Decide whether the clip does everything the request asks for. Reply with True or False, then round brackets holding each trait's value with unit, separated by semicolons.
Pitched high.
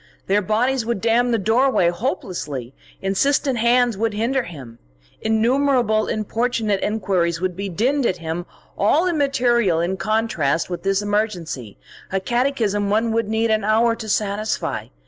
True (215 Hz)